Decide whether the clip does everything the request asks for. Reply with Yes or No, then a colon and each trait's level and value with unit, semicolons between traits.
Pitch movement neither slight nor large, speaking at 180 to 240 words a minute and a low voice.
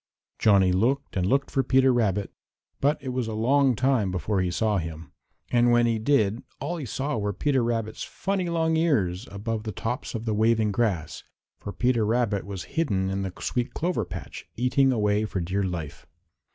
Yes: average, 4.7 semitones; average, 190 wpm; low, 115 Hz